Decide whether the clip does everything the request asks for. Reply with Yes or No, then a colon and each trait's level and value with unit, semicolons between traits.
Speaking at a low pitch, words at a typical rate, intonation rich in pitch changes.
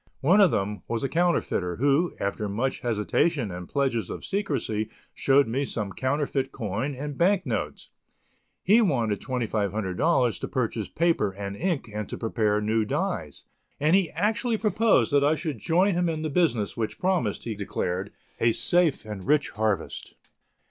Yes: low, 130 Hz; average, 160 wpm; wide, 7.6 semitones